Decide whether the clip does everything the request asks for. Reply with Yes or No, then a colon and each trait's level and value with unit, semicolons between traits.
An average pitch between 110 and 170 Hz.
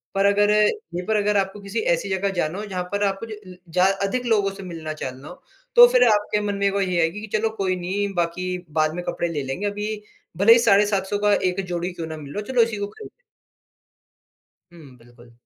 No: high, 195 Hz